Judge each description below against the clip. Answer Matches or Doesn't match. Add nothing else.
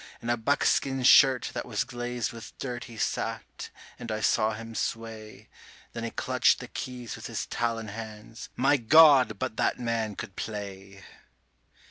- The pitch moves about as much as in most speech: Doesn't match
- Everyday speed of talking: Matches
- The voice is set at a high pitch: Doesn't match